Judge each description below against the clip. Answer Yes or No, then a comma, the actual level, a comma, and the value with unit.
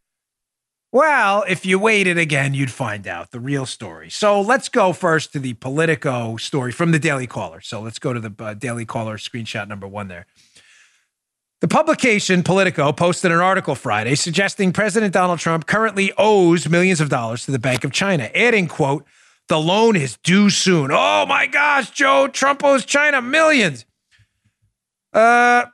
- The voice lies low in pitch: No, medium, 165 Hz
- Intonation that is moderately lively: No, wide, 7.9 semitones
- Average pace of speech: Yes, average, 170 wpm